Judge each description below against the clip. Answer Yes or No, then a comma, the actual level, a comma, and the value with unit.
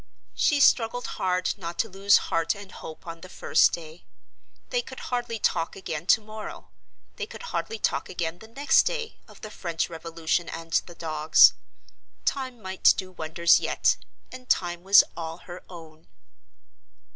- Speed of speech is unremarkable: Yes, average, 160 wpm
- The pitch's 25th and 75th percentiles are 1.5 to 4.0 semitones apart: No, average, 5.2 semitones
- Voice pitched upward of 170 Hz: Yes, medium, 185 Hz